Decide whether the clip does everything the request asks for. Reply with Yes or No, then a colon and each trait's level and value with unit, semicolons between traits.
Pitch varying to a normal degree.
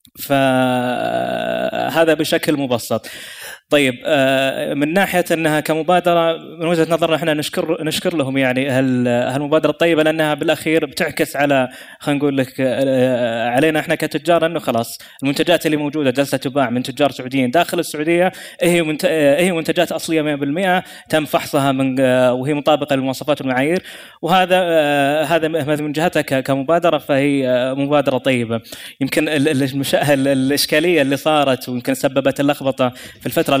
Yes: average, 3.2 semitones